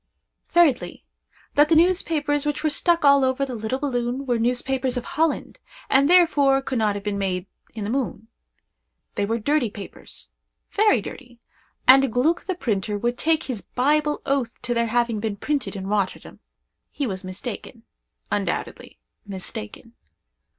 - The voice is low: No, very high, 255 Hz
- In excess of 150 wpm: No, average, 145 wpm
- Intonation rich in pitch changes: No, average, 4.9 semitones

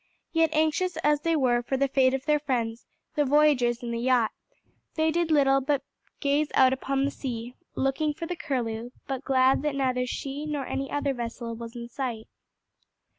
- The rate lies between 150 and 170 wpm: No, average, 185 wpm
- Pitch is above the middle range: Yes, very high, 270 Hz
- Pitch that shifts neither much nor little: Yes, average, 3.3 semitones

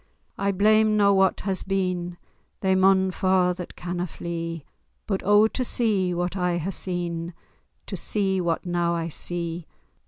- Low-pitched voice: No, medium, 185 Hz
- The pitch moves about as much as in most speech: No, narrow, 2.0 semitones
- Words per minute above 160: No, average, 155 wpm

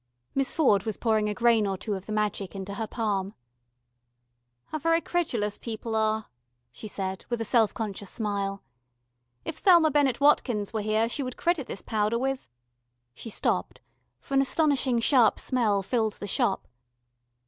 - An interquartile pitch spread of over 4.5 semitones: No, average, 4.1 semitones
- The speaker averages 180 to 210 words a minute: No, average, 170 wpm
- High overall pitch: Yes, high, 220 Hz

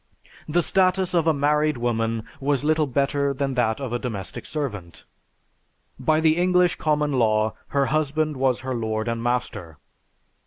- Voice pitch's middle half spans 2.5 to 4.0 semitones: No, average, 4.7 semitones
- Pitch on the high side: No, medium, 140 Hz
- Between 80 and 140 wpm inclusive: No, average, 155 wpm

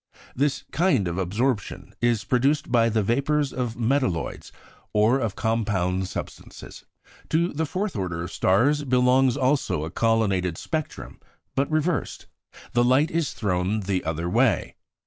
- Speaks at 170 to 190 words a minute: No, average, 140 wpm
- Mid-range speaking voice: No, low, 120 Hz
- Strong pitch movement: Yes, wide, 6.4 semitones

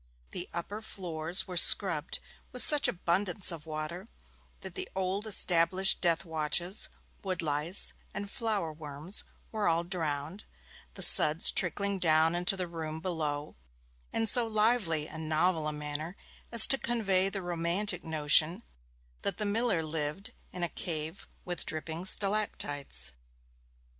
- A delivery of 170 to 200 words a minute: No, average, 140 wpm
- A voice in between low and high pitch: Yes, medium, 175 Hz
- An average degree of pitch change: Yes, average, 3.9 semitones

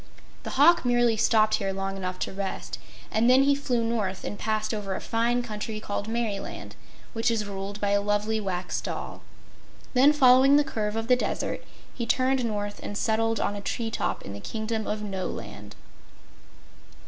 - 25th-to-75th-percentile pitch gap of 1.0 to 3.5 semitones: Yes, average, 2.9 semitones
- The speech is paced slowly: No, average, 180 wpm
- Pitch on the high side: Yes, high, 220 Hz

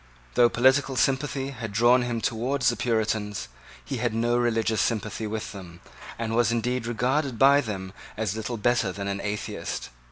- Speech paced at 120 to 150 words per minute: No, average, 165 wpm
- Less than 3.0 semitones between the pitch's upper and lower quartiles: Yes, narrow, 2.6 semitones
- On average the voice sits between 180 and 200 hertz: No, low, 115 Hz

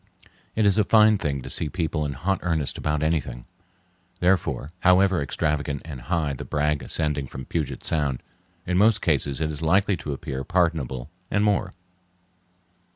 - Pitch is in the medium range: No, very low, 80 Hz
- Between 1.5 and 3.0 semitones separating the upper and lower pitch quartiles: No, average, 4.3 semitones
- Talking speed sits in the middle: Yes, average, 160 wpm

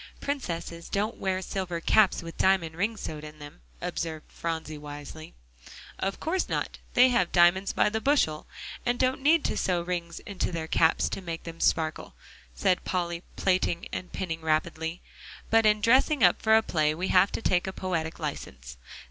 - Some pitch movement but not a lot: Yes, average, 4.2 semitones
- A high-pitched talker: No, medium, 175 Hz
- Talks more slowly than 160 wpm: No, average, 175 wpm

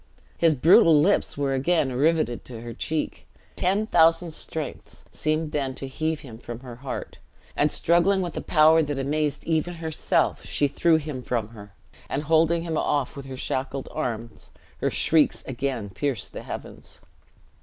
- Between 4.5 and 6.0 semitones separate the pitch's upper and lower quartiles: No, average, 3.7 semitones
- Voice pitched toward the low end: No, medium, 150 Hz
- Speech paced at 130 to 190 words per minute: Yes, average, 165 wpm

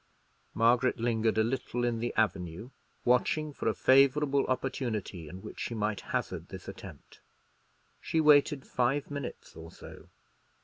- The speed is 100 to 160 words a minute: Yes, average, 140 wpm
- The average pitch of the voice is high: No, low, 120 Hz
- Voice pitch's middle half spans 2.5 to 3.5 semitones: No, average, 3.9 semitones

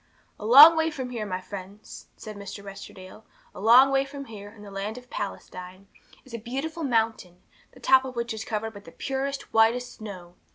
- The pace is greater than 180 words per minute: Yes, average, 200 wpm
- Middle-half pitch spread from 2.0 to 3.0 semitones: No, average, 4.5 semitones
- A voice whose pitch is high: Yes, high, 225 Hz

